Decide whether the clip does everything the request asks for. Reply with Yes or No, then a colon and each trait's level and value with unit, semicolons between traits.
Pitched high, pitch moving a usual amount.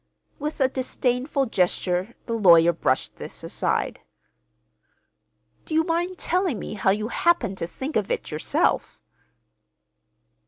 No: high, 235 Hz; wide, 8.3 semitones